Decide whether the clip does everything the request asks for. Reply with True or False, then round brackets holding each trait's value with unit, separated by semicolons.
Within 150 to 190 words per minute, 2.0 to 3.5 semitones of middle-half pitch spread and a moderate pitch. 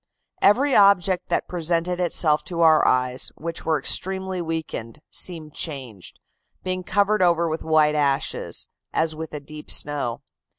False (140 wpm; 3.2 semitones; 160 Hz)